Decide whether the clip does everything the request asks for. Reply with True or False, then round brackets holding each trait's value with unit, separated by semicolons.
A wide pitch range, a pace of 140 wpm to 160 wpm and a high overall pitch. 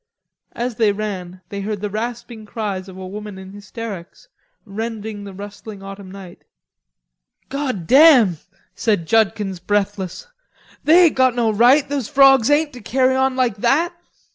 False (4.5 semitones; 150 wpm; 215 Hz)